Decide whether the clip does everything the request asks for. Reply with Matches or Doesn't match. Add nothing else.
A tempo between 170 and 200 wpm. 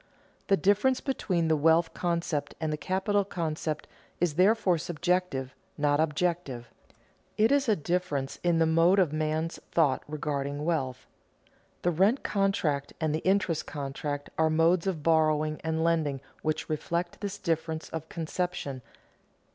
Doesn't match